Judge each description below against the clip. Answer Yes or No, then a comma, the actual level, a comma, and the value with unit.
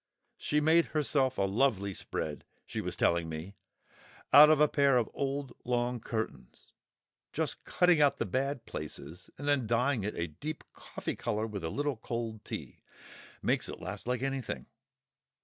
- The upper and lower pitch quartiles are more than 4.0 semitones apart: Yes, average, 5.3 semitones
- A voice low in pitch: Yes, low, 125 Hz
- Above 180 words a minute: No, average, 165 wpm